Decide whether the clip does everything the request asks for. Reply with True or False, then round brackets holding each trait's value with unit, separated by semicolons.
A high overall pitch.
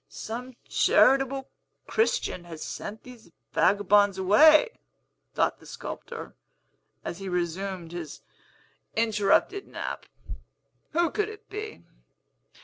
True (220 Hz)